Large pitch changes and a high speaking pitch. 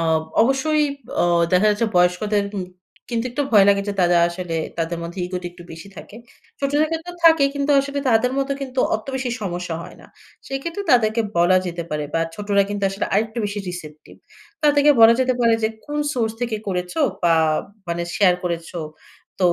Yes: wide, 6.7 semitones; high, 210 Hz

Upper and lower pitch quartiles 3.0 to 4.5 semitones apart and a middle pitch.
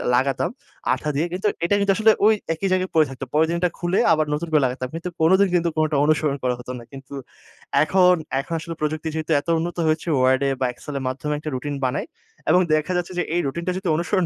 Yes: average, 3.9 semitones; medium, 155 Hz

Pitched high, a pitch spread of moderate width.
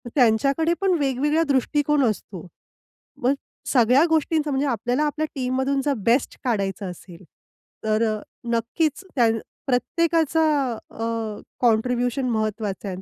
Yes: very high, 250 Hz; average, 4.9 semitones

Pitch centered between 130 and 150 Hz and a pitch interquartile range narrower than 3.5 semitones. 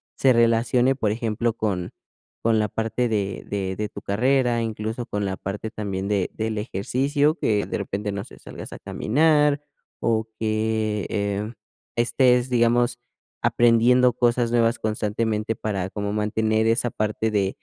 No: low, 110 Hz; narrow, 2.4 semitones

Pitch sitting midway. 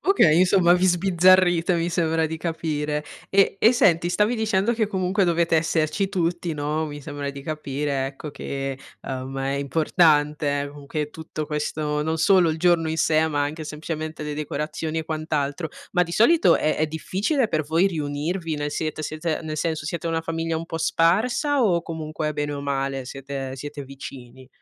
Yes: medium, 155 Hz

